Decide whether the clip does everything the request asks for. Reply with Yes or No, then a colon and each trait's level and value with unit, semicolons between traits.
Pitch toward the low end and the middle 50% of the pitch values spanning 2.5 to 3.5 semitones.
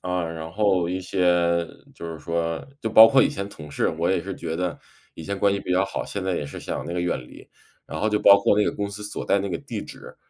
Yes: very low, 90 Hz; average, 3.0 semitones